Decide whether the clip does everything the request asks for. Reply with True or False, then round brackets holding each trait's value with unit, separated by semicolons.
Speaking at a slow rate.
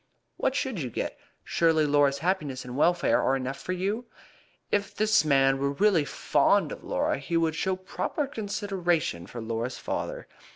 False (165 wpm)